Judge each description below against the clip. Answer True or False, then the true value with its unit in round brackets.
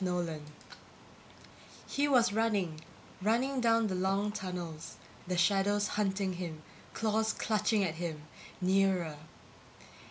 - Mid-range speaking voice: False (195 Hz)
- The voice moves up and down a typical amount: True (3.5 semitones)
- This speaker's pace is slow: True (105 wpm)